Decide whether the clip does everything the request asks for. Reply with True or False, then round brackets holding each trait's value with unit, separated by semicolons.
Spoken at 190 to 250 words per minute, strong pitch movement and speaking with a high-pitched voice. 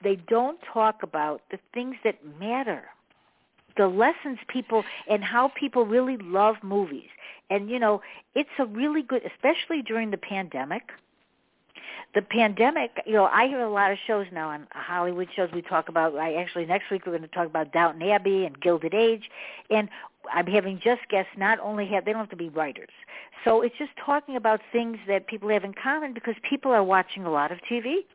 False (195 wpm; 4.3 semitones; 210 Hz)